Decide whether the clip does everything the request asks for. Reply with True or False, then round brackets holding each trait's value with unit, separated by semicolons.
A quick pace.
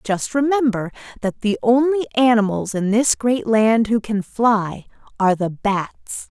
False (150 wpm)